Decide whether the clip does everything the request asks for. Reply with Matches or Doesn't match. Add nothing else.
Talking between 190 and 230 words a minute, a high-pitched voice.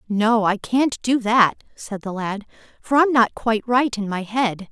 Matches